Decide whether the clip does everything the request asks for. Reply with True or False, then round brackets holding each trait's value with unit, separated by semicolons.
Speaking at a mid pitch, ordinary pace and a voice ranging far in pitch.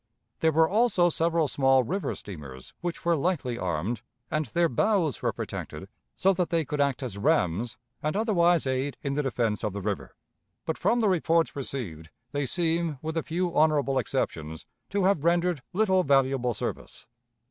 True (150 Hz; 170 wpm; 6.0 semitones)